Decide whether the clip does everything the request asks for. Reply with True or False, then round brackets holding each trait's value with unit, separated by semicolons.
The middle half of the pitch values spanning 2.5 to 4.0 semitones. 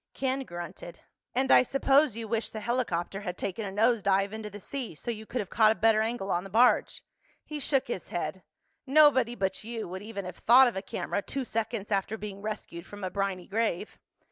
True (3.7 semitones)